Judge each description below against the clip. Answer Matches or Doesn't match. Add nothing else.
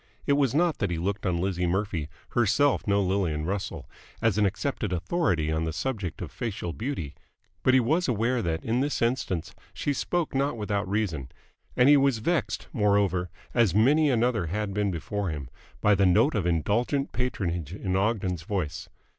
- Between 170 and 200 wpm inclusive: Matches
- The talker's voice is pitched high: Doesn't match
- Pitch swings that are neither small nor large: Doesn't match